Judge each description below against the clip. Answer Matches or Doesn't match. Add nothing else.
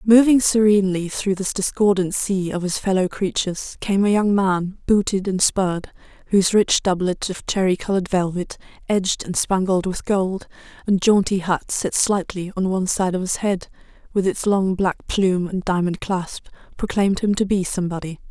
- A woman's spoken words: Matches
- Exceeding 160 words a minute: Matches